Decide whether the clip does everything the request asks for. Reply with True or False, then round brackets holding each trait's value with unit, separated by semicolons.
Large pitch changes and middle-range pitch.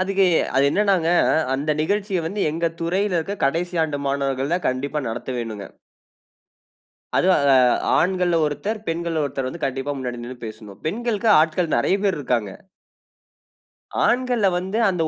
True (5.9 semitones; 165 Hz)